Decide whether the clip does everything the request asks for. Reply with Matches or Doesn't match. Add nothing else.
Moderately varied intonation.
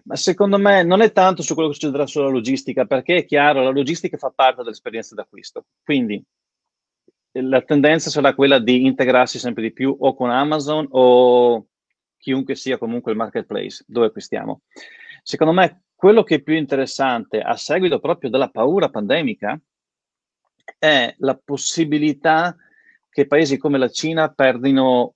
Matches